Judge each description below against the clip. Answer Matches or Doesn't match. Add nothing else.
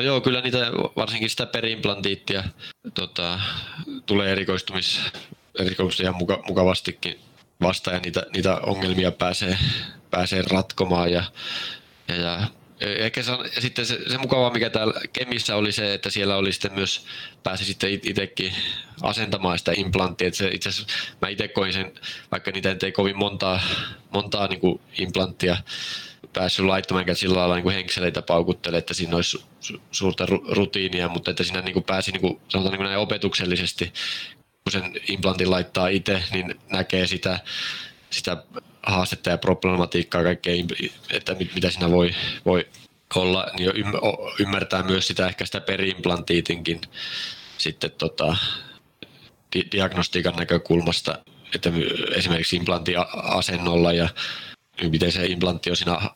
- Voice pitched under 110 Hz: Matches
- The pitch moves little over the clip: Matches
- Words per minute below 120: Doesn't match